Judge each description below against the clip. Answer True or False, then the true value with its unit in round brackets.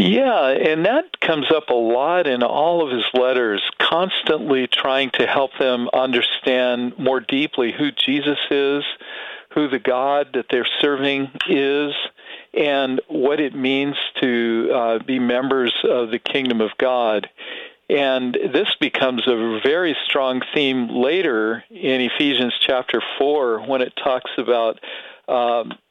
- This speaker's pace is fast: False (140 wpm)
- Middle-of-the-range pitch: False (130 Hz)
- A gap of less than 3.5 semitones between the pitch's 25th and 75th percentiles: True (2.8 semitones)